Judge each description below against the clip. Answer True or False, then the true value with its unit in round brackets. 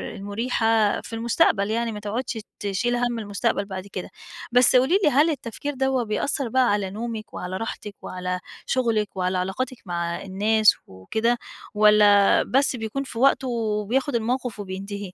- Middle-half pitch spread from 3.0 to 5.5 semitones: True (3.5 semitones)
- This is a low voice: False (220 Hz)